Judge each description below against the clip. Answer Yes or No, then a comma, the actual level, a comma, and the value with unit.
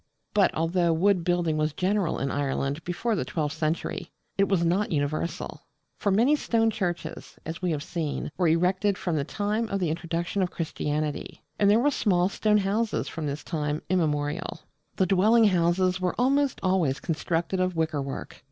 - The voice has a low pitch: No, medium, 175 Hz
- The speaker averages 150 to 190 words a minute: Yes, average, 170 wpm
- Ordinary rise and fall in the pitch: Yes, average, 4.0 semitones